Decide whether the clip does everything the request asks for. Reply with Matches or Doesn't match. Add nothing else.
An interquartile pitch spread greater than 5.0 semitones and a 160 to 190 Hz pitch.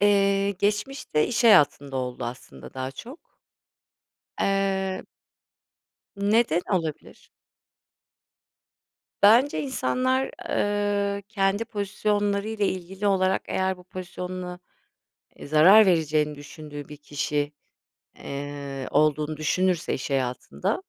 Matches